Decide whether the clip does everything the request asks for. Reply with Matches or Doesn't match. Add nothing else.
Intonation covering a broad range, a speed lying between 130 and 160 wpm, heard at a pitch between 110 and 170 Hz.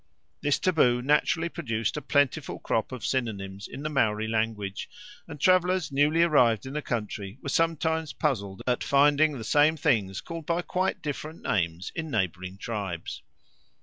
Matches